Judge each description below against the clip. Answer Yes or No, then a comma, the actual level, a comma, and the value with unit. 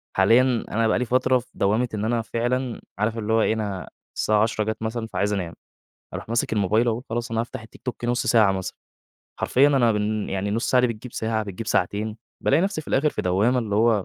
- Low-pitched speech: Yes, low, 110 Hz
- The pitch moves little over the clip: Yes, narrow, 2.3 semitones